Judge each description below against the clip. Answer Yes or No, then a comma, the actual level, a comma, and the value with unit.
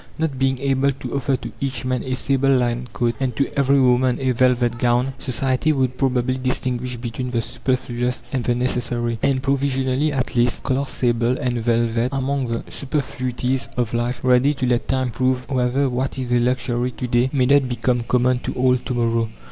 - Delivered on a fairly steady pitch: Yes, narrow, 1.5 semitones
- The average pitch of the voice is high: No, low, 125 Hz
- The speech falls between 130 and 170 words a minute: No, average, 190 wpm